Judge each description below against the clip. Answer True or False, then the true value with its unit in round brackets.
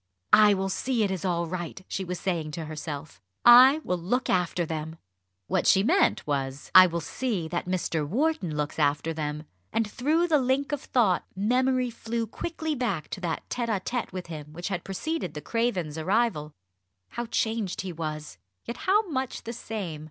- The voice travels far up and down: True (6.9 semitones)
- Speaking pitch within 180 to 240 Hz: True (190 Hz)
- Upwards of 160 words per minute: True (185 wpm)